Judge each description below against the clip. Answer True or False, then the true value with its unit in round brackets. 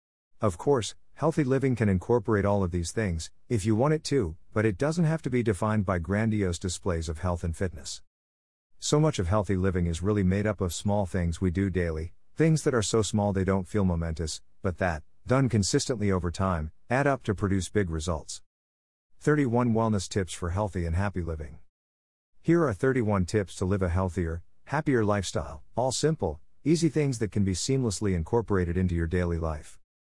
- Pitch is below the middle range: True (95 Hz)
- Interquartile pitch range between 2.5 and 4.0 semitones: False (4.7 semitones)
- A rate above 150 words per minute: True (190 wpm)